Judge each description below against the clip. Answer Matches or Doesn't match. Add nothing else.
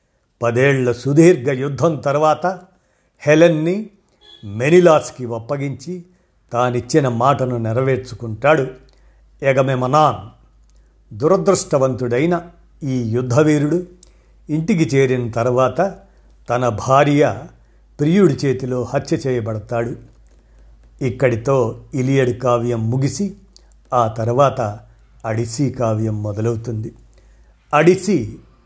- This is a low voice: Matches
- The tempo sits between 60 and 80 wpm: Matches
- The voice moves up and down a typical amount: Matches